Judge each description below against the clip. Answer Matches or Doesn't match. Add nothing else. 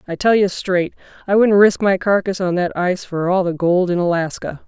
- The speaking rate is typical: Doesn't match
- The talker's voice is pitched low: Doesn't match